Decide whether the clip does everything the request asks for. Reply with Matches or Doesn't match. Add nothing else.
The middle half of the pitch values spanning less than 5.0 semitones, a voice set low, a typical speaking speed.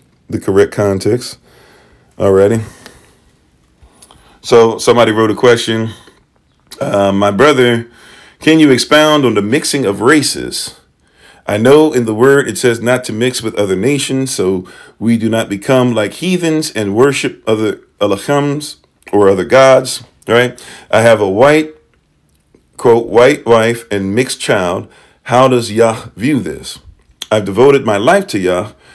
Matches